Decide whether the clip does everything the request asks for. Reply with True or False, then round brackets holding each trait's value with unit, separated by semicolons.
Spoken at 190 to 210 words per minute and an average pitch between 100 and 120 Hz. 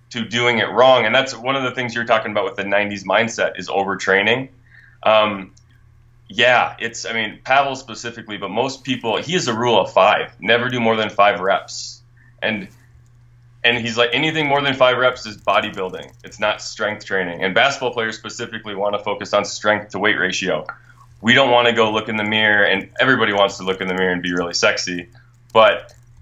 True (205 wpm; 115 Hz)